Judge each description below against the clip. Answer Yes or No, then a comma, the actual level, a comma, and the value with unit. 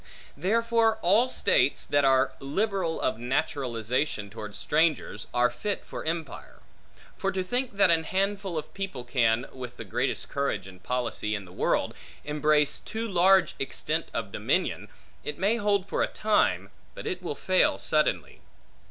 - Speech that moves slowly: No, average, 155 wpm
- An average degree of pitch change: No, wide, 7.8 semitones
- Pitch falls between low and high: Yes, medium, 155 Hz